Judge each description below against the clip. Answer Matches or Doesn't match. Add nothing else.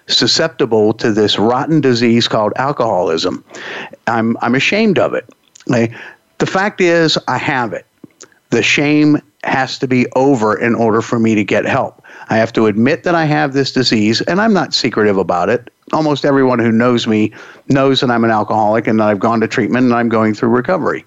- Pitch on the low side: Matches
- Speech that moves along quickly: Doesn't match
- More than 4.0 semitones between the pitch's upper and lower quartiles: Matches